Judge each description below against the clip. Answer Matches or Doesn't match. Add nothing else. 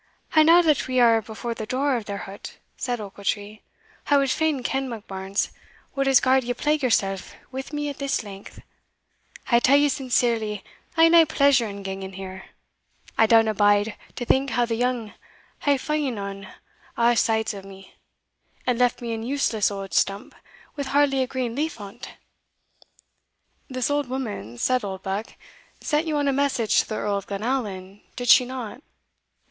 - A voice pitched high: Matches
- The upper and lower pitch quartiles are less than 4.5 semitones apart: Doesn't match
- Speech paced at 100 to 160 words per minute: Doesn't match